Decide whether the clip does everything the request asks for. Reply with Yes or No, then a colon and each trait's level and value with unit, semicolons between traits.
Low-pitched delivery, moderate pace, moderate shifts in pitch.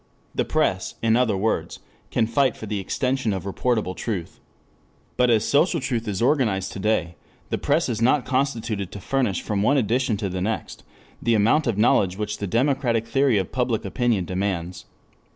Yes: low, 110 Hz; average, 180 wpm; average, 4.3 semitones